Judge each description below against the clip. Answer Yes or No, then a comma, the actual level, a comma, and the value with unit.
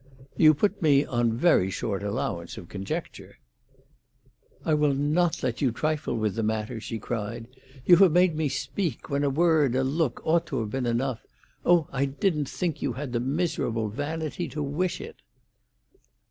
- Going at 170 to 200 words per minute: Yes, average, 175 wpm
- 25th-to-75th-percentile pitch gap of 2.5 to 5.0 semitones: No, wide, 5.5 semitones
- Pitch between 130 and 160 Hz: Yes, medium, 140 Hz